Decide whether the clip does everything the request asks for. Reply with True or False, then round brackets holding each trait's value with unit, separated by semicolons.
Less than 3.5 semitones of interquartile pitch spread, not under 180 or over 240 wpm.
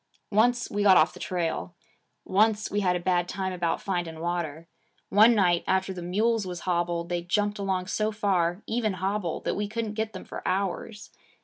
True (3.1 semitones; 190 wpm)